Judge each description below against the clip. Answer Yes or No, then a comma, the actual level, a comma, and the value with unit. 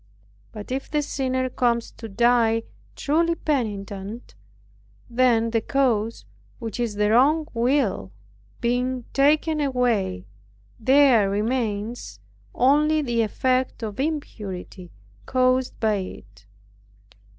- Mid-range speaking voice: No, high, 240 Hz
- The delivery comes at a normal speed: No, slow, 105 wpm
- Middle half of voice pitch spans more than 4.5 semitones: No, average, 3.8 semitones